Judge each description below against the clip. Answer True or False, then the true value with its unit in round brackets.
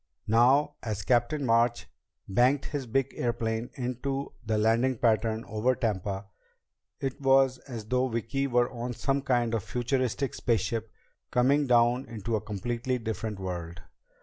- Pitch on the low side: True (120 Hz)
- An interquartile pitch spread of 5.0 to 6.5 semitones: False (2.8 semitones)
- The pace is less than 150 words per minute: True (140 wpm)